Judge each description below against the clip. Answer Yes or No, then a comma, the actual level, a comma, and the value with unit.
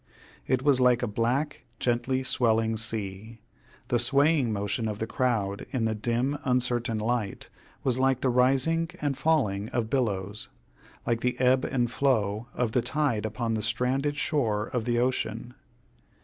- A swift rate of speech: No, average, 155 wpm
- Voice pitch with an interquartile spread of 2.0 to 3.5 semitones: Yes, average, 2.9 semitones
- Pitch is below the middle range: Yes, low, 120 Hz